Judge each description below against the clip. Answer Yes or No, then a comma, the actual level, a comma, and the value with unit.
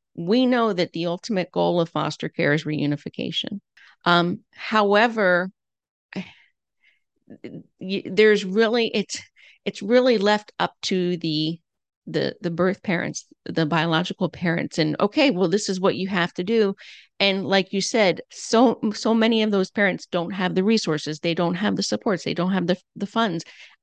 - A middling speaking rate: Yes, average, 160 wpm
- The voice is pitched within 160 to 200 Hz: Yes, high, 190 Hz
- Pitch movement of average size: Yes, average, 4.1 semitones